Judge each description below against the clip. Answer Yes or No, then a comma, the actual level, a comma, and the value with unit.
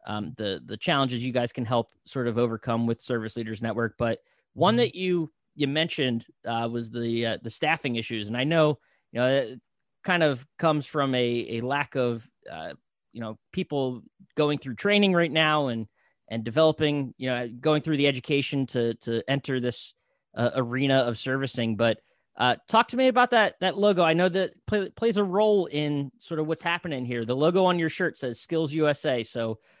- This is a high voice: No, low, 135 Hz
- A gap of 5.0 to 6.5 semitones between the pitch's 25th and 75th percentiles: Yes, average, 5.3 semitones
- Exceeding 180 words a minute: Yes, average, 200 wpm